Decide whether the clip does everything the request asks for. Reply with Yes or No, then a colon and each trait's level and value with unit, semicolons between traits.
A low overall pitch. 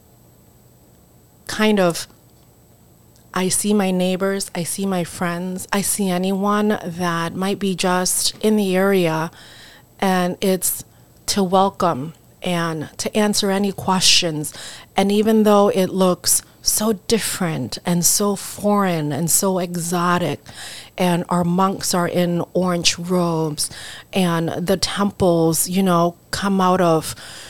No: medium, 180 Hz